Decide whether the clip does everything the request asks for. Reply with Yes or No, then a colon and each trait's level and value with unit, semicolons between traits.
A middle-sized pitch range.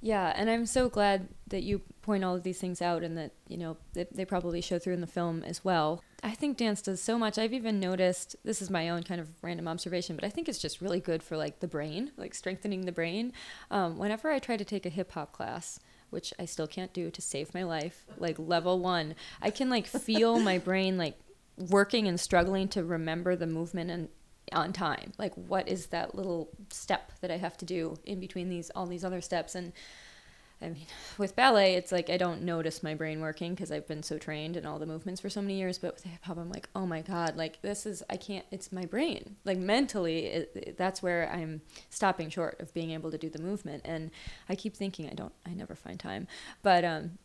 Yes: average, 3.0 semitones